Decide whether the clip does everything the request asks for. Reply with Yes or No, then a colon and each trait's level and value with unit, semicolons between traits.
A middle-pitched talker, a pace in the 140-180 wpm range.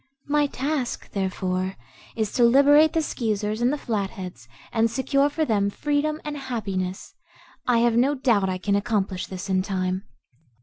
No: high, 225 Hz; average, 160 wpm